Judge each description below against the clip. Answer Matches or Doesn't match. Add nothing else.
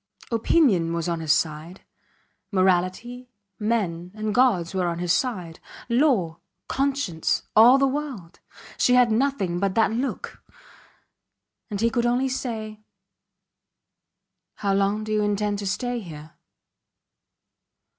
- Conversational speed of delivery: Doesn't match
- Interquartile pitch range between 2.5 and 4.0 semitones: Doesn't match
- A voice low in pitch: Doesn't match